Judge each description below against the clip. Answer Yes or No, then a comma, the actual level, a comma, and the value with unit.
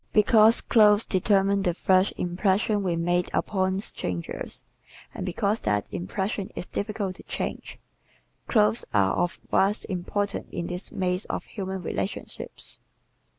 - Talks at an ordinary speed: No, slow, 130 wpm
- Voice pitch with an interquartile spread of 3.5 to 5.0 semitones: No, narrow, 2.6 semitones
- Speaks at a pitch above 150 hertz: Yes, high, 190 Hz